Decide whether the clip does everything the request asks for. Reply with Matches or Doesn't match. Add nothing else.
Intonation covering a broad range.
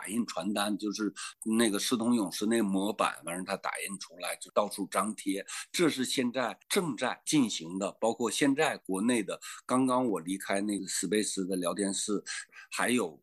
Doesn't match